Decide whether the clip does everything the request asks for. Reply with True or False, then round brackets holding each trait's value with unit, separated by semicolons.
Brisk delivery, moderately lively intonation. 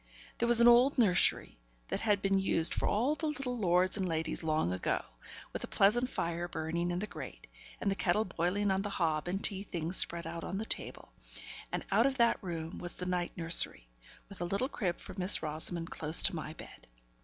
True (210 wpm; 3.8 semitones)